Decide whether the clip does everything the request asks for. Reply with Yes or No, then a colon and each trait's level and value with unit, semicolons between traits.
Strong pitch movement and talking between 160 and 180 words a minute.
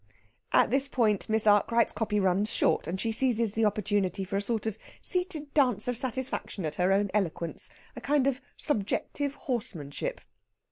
No: average, 4.4 semitones; average, 170 wpm